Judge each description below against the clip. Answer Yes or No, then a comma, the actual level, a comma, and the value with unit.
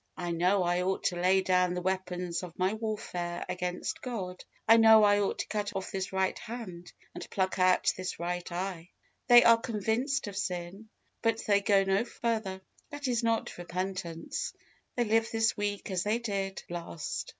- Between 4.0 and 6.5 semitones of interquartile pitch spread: No, average, 3.5 semitones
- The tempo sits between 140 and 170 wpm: No, average, 180 wpm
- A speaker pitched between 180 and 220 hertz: Yes, high, 190 Hz